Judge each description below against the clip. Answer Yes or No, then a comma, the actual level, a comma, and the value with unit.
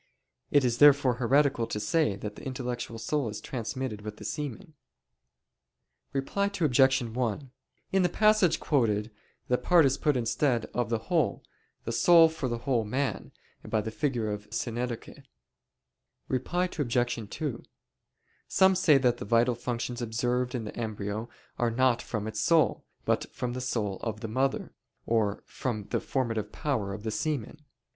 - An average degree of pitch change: Yes, average, 4.1 semitones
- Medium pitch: No, low, 125 Hz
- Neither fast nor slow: Yes, average, 160 wpm